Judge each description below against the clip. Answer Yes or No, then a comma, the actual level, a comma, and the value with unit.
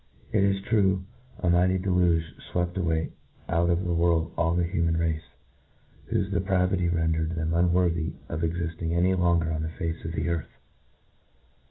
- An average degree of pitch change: No, narrow, 1.6 semitones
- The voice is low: Yes, very low, 85 Hz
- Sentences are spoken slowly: No, average, 175 wpm